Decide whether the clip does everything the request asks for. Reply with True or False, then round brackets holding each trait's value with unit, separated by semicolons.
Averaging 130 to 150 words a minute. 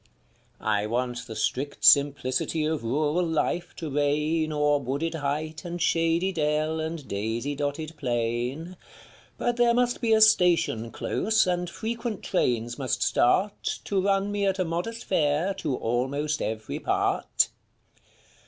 True (140 wpm)